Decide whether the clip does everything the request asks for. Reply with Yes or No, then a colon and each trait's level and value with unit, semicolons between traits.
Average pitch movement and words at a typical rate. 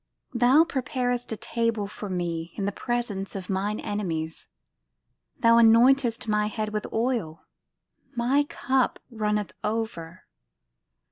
No: average, 3.5 semitones; slow, 120 wpm